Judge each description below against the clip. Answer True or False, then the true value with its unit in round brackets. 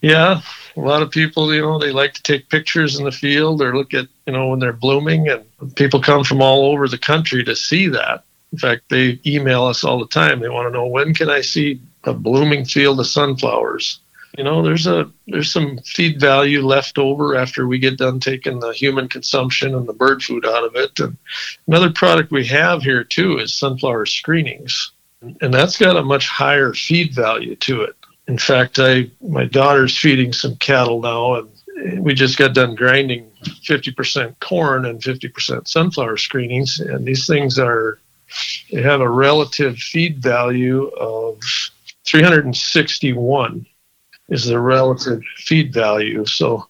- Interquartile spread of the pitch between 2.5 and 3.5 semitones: True (2.8 semitones)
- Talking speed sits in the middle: True (180 wpm)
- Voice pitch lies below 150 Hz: True (135 Hz)